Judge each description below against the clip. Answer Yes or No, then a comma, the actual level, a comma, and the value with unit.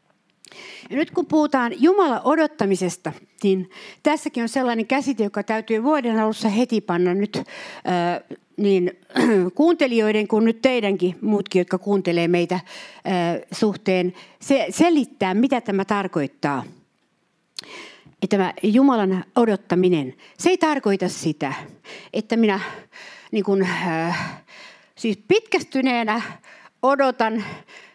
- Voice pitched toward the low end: No, high, 215 Hz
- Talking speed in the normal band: Yes, average, 110 wpm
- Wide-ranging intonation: Yes, wide, 6.2 semitones